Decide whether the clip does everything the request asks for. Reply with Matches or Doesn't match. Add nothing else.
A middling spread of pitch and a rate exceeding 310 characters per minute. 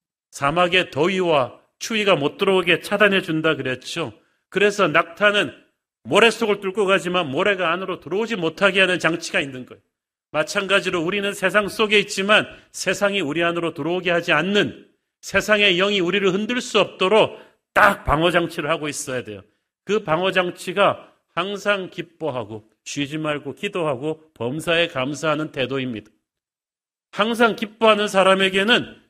Matches